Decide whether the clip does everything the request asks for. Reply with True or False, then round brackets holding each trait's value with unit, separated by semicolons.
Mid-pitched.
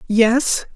False (235 Hz)